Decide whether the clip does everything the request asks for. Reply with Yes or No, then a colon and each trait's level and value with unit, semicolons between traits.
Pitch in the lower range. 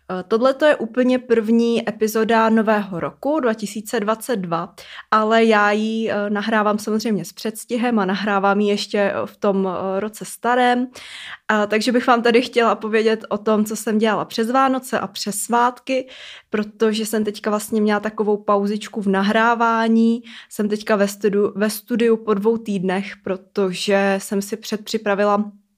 No: high, 215 Hz